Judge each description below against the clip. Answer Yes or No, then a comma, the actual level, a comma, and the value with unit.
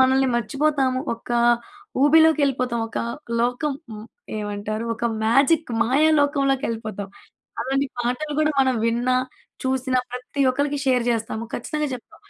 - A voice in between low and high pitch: No, very high, 260 Hz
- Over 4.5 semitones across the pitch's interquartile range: No, average, 3.1 semitones